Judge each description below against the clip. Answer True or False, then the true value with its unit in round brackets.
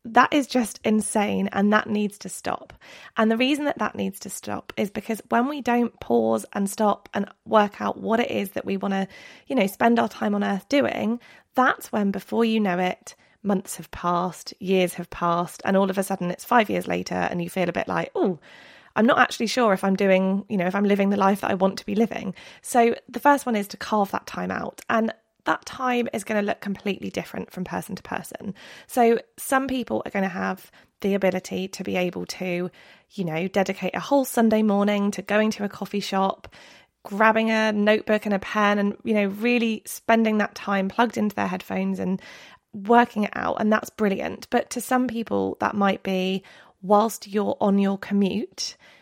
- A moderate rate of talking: False (215 wpm)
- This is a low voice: False (205 Hz)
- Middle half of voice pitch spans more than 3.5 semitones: False (2.9 semitones)